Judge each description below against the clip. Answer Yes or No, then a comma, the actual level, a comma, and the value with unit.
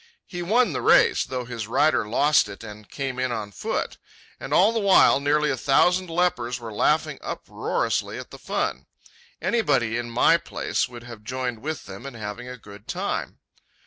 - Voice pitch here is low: Yes, low, 125 Hz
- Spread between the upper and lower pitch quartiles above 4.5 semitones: Yes, average, 5.3 semitones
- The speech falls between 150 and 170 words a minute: No, average, 180 wpm